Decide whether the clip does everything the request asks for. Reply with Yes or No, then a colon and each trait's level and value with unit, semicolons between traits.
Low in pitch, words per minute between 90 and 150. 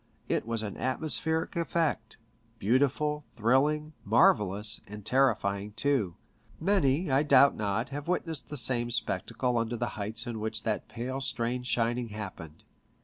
Yes: low, 120 Hz; average, 140 wpm